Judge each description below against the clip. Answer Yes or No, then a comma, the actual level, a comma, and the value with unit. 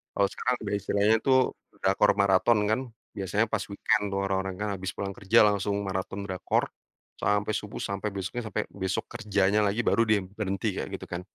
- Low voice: Yes, low, 100 Hz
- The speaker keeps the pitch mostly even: Yes, narrow, 1.8 semitones